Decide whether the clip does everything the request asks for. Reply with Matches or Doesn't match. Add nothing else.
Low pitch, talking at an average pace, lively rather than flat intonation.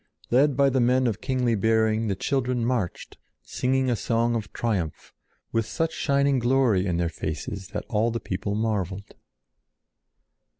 Doesn't match